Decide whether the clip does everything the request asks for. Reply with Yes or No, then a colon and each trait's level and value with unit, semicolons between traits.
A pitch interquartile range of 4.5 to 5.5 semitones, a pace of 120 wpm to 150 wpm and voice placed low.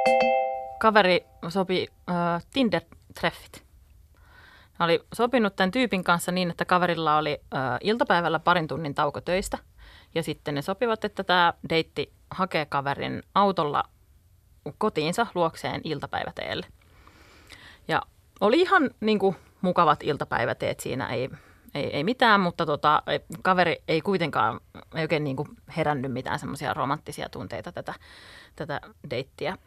No: average, 5.1 semitones; average, 125 wpm; medium, 165 Hz